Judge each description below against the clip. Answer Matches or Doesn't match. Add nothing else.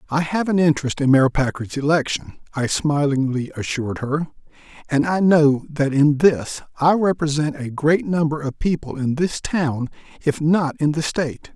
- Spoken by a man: Matches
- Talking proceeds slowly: Doesn't match